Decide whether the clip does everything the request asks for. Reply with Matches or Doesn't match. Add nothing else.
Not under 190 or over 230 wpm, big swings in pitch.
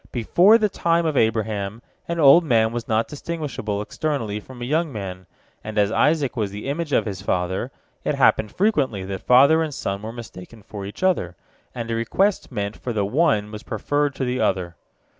Matches